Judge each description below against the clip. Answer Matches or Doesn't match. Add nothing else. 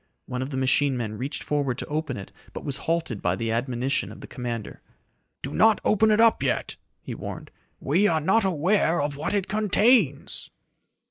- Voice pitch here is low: Doesn't match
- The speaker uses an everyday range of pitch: Doesn't match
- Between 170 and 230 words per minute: Matches